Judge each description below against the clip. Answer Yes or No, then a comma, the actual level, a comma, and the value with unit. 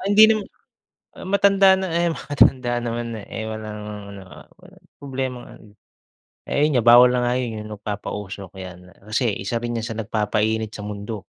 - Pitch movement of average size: Yes, average, 3.7 semitones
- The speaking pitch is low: Yes, low, 115 Hz